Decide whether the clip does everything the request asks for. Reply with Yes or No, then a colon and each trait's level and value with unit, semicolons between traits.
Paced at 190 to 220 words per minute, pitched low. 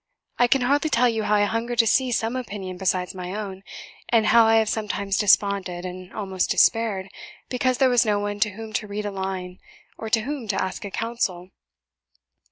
No: average, 200 wpm; high, 210 Hz